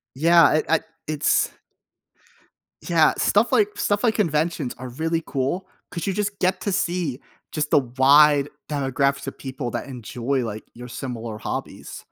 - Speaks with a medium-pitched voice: Yes, medium, 150 Hz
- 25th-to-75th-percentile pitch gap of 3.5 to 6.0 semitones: Yes, average, 4.7 semitones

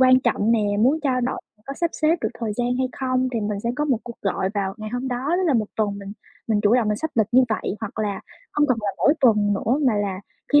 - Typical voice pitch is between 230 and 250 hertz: Yes, high, 235 Hz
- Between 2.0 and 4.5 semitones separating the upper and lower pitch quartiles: Yes, average, 3.8 semitones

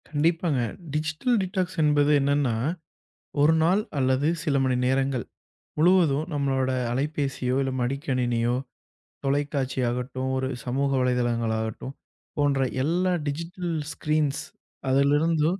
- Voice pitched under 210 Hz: Yes, medium, 140 Hz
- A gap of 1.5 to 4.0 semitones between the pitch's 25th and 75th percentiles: Yes, average, 3.1 semitones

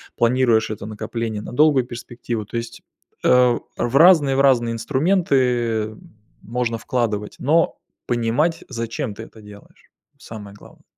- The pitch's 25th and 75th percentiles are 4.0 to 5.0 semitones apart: No, average, 2.9 semitones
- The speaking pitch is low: Yes, low, 120 Hz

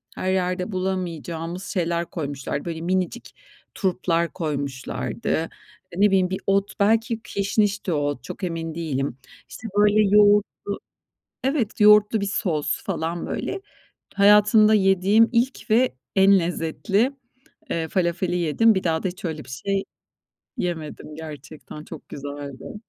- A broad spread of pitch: No, average, 4.1 semitones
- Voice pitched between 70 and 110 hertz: No, medium, 185 Hz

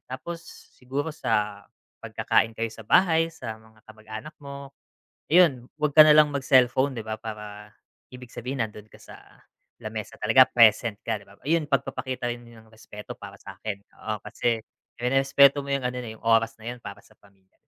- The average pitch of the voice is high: No, low, 120 Hz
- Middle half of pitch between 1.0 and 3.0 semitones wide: No, average, 4.1 semitones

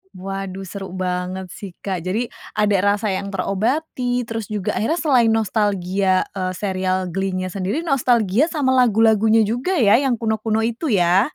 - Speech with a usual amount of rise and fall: Yes, average, 3.7 semitones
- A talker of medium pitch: No, high, 205 Hz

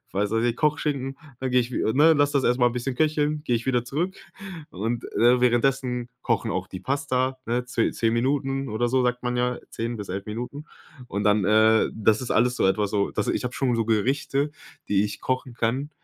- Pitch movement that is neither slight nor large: Yes, average, 3.2 semitones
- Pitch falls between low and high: No, low, 125 Hz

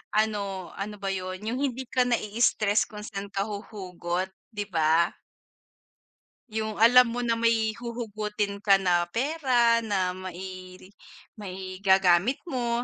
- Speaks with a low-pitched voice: No, high, 210 Hz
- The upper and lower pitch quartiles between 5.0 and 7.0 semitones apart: No, average, 3.7 semitones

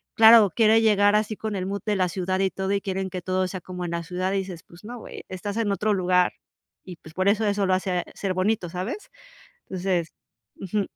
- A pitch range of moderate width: No, narrow, 2.2 semitones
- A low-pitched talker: No, high, 190 Hz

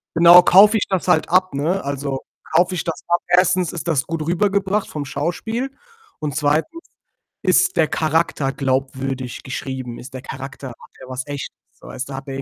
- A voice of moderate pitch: Yes, medium, 155 Hz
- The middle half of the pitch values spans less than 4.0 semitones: No, average, 5.1 semitones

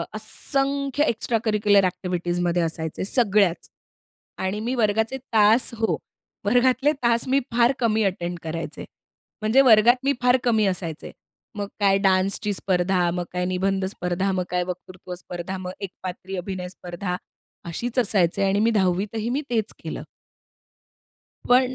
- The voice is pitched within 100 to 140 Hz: No, high, 200 Hz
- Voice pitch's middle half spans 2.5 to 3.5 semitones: No, average, 4.2 semitones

